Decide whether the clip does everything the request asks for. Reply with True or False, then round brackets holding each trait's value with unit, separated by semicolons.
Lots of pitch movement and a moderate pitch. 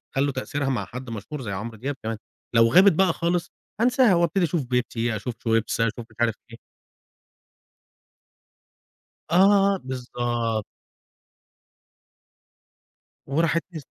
False (6.6 semitones; 130 Hz)